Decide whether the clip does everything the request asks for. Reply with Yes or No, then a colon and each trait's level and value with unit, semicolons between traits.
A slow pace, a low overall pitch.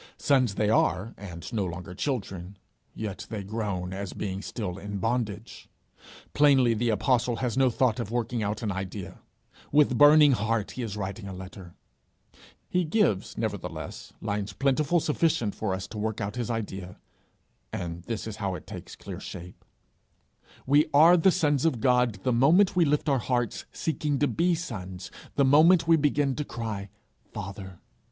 No: average, 170 wpm; low, 115 Hz